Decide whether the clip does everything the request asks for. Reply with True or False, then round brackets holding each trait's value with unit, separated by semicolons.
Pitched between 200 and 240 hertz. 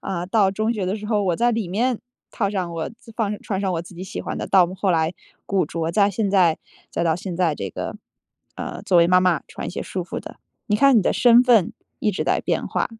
False (190 Hz)